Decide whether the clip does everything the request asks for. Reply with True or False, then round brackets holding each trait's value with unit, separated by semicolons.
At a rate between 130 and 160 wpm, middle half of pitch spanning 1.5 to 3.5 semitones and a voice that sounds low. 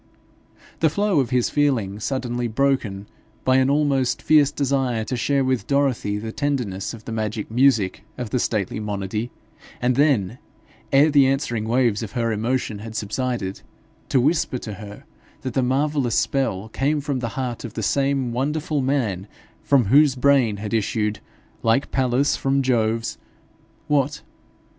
False (155 wpm; 4.0 semitones; 125 Hz)